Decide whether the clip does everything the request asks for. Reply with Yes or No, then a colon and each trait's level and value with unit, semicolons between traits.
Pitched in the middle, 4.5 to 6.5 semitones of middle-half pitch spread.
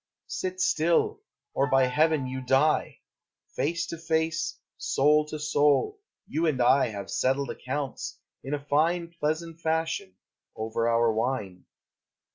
No: medium, 145 Hz; average, 3.9 semitones